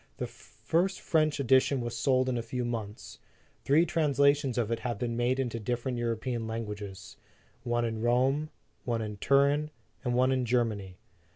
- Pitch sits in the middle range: No, low, 120 Hz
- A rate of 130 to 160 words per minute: No, average, 170 wpm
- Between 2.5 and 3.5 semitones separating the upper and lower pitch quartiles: Yes, average, 2.9 semitones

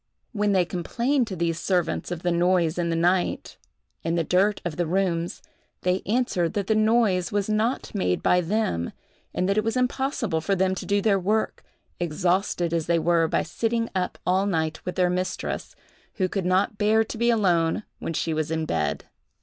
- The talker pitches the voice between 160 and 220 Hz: Yes, medium, 185 Hz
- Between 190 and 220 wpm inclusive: Yes, average, 195 wpm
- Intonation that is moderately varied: Yes, average, 3.6 semitones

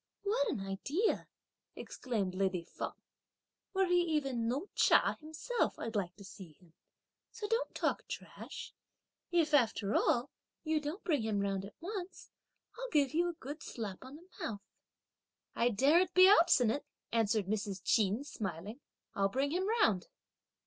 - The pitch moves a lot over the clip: Yes, wide, 9.0 semitones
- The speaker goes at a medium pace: Yes, average, 150 wpm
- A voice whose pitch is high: Yes, very high, 260 Hz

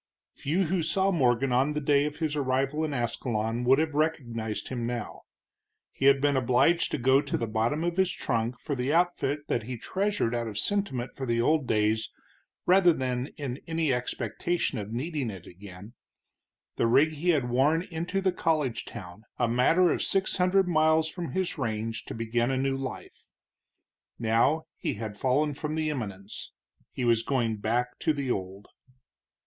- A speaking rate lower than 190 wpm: Yes, average, 180 wpm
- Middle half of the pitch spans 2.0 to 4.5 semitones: No, average, 5.3 semitones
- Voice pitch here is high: No, low, 135 Hz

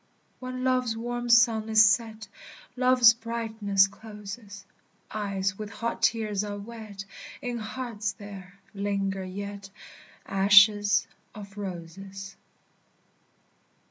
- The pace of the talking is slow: Yes, slow, 100 wpm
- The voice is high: Yes, high, 210 Hz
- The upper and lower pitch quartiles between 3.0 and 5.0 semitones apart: No, narrow, 2.5 semitones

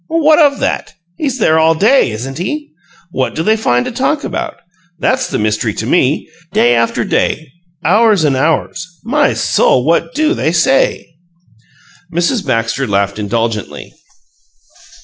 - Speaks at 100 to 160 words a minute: Yes, average, 150 wpm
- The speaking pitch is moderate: Yes, medium, 165 Hz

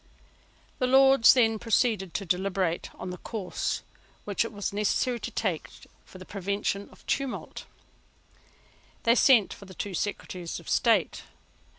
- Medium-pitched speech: No, high, 205 Hz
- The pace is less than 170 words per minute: Yes, average, 145 wpm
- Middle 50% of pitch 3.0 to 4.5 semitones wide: Yes, average, 3.8 semitones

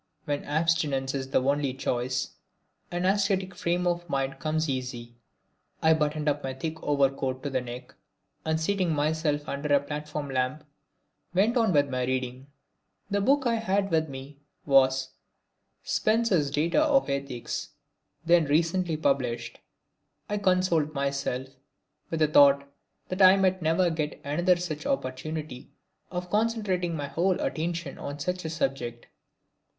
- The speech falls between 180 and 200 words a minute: No, average, 145 wpm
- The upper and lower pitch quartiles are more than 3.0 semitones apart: Yes, average, 4.5 semitones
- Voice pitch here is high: No, medium, 155 Hz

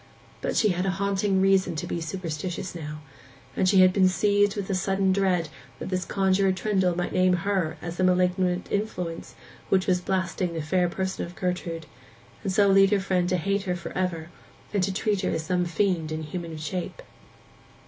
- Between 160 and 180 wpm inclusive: No, average, 190 wpm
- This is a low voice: No, medium, 185 Hz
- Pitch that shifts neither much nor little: No, narrow, 1.8 semitones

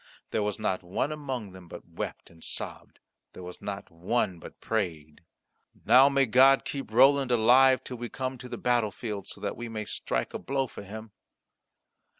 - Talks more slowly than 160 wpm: No, average, 180 wpm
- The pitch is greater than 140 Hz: No, low, 115 Hz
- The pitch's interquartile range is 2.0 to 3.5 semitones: No, average, 5.2 semitones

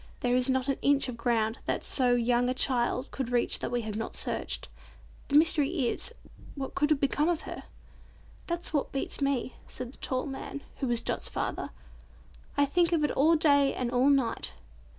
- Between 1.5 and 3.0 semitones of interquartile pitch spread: Yes, average, 2.7 semitones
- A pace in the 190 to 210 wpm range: Yes, average, 195 wpm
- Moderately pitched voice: No, very high, 270 Hz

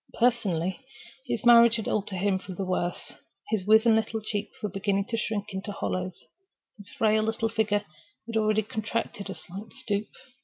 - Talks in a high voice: Yes, high, 210 Hz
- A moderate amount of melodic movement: No, narrow, 2.2 semitones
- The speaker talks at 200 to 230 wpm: No, average, 165 wpm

